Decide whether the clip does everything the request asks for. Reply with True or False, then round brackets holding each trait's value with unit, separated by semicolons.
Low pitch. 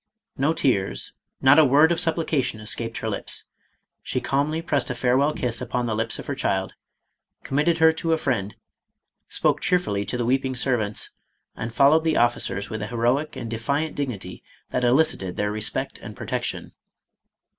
True (125 Hz)